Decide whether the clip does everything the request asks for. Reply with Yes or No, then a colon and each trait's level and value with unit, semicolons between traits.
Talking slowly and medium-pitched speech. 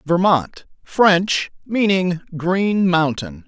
Yes: slow, 70 wpm; medium, 180 Hz